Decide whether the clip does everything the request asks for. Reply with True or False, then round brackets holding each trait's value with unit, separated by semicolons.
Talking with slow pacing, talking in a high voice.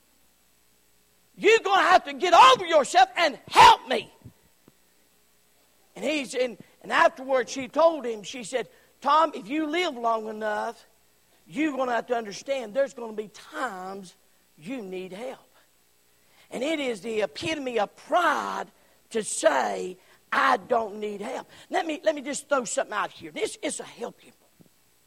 False (165 wpm; 235 Hz)